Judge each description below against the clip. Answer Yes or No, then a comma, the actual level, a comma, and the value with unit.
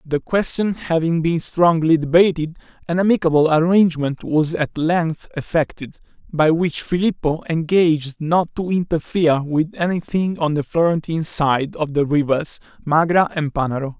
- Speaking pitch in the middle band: Yes, medium, 160 Hz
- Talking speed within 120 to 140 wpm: Yes, slow, 135 wpm